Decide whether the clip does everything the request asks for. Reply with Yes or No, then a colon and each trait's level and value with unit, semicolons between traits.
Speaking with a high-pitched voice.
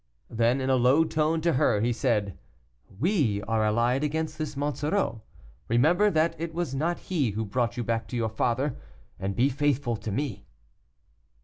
No: low, 130 Hz